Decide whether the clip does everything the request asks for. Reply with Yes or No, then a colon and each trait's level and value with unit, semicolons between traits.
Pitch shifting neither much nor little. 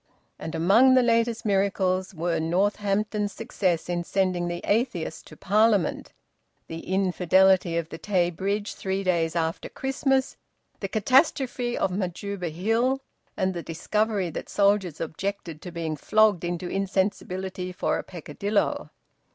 Yes: average, 3.3 semitones